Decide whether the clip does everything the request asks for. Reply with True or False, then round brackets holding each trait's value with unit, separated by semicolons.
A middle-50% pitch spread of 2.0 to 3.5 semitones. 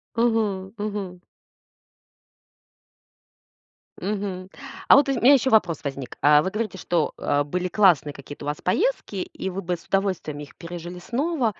False (4.3 semitones)